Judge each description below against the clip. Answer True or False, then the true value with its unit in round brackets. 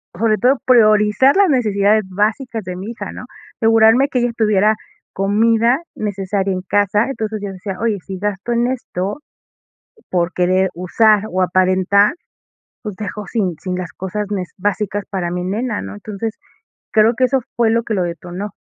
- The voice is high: True (210 Hz)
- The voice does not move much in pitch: False (3.1 semitones)